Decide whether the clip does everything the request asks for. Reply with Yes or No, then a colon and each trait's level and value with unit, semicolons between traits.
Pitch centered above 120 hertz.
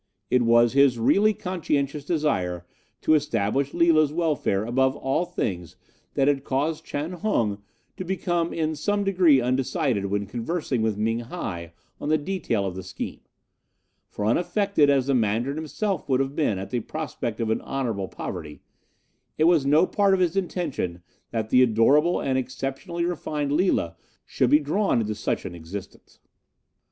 Yes: low, 135 Hz